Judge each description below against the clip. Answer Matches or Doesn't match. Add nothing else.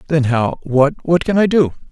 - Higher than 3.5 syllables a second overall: Matches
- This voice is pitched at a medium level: Matches